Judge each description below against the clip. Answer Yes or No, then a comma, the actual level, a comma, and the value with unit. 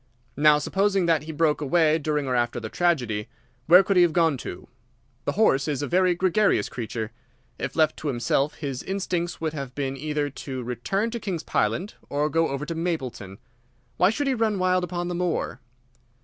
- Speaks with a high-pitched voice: No, medium, 160 Hz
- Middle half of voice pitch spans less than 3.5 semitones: No, average, 4.7 semitones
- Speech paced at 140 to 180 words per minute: No, average, 190 wpm